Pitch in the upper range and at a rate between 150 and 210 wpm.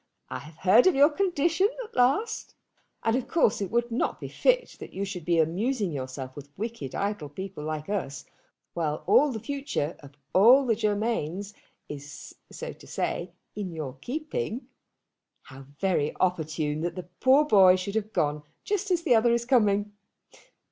Yes: high, 200 Hz; average, 170 wpm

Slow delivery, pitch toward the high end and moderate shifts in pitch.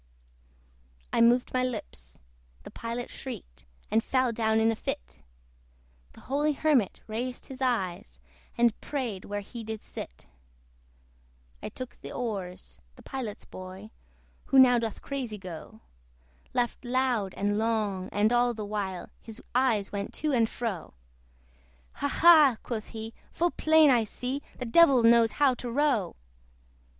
No: average, 145 wpm; high, 230 Hz; average, 3.8 semitones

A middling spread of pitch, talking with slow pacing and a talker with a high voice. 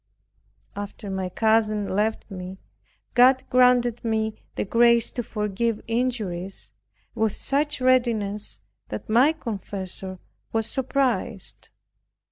Yes: average, 3.3 semitones; slow, 100 wpm; high, 220 Hz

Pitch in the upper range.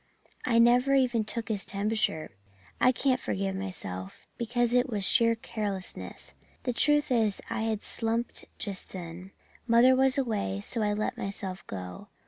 Yes: high, 220 Hz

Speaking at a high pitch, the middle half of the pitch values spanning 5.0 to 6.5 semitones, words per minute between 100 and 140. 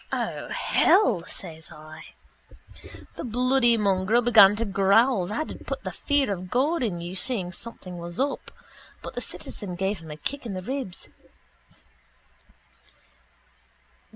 Yes: high, 200 Hz; wide, 5.6 semitones; slow, 135 wpm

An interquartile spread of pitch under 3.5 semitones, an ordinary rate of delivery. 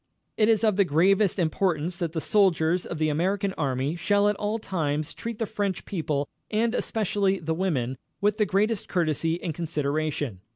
No: average, 4.7 semitones; average, 175 wpm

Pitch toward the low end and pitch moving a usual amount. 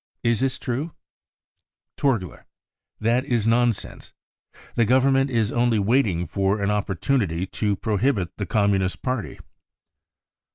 Yes: low, 115 Hz; average, 4.1 semitones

